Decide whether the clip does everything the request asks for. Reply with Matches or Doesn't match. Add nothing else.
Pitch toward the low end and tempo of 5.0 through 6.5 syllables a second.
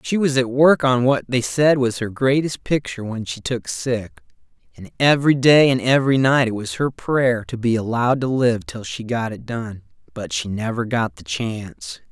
Doesn't match